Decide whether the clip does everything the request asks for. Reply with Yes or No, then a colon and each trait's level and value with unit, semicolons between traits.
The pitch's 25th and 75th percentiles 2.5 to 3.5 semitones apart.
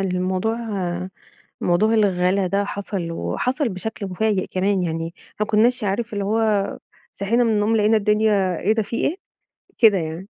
Yes: average, 2.9 semitones